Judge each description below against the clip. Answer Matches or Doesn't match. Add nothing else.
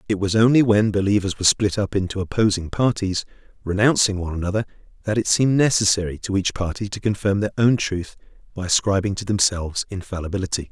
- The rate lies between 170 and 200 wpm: Matches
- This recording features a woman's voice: Doesn't match